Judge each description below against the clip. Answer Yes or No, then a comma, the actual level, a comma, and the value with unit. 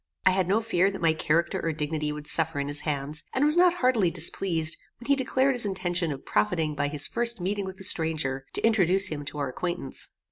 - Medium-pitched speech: Yes, medium, 170 Hz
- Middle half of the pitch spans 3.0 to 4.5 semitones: No, average, 4.9 semitones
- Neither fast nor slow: No, fast, 225 wpm